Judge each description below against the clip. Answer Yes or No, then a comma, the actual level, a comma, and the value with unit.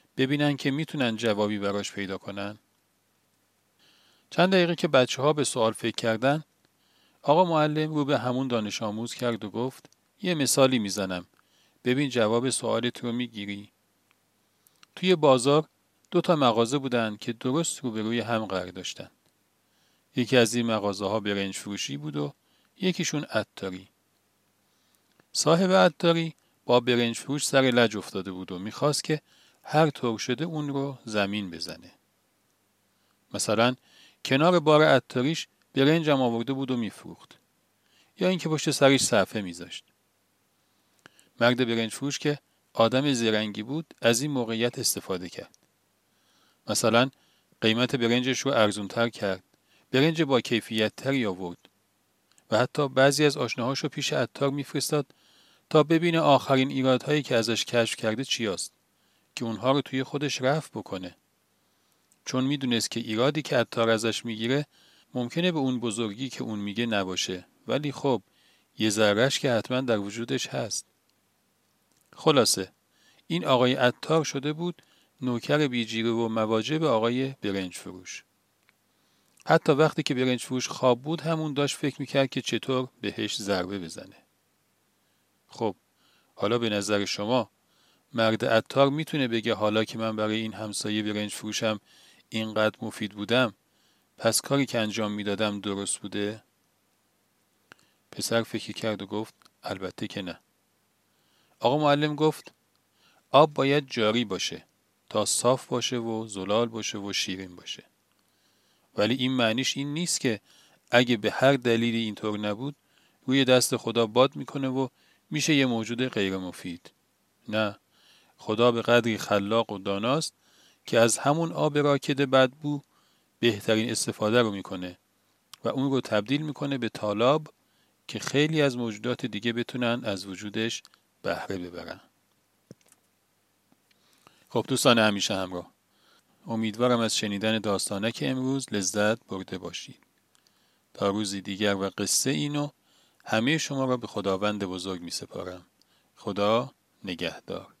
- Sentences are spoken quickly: No, average, 135 wpm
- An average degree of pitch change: Yes, average, 4.8 semitones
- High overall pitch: No, low, 120 Hz